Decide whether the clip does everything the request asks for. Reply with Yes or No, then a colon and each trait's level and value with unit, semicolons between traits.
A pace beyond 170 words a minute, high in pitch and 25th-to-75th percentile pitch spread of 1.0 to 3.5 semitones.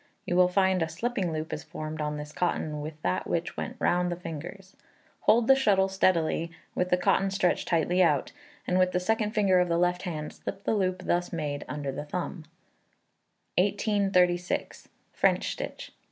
No: average, 180 wpm; medium, 180 Hz; average, 3.2 semitones